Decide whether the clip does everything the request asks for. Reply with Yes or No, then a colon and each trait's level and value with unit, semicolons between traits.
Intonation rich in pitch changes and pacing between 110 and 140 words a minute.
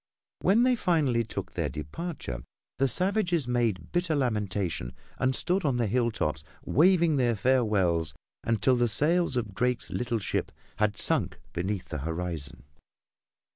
Yes: wide, 8.0 semitones; slow, 135 wpm